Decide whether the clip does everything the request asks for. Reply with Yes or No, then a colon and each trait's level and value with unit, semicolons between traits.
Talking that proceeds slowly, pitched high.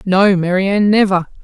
Yes: slow, 125 wpm; high, 195 Hz